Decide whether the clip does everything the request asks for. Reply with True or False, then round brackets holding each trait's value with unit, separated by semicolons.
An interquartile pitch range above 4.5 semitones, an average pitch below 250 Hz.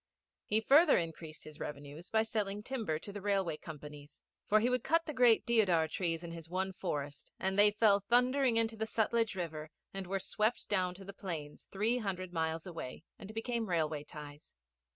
True (5.5 semitones; 190 Hz)